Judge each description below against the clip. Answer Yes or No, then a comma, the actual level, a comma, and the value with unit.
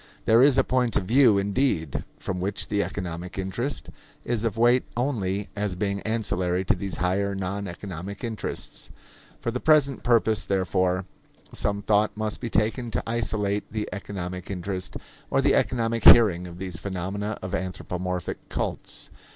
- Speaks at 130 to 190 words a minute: Yes, average, 155 wpm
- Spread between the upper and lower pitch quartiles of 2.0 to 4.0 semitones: Yes, average, 3.6 semitones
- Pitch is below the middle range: Yes, low, 100 Hz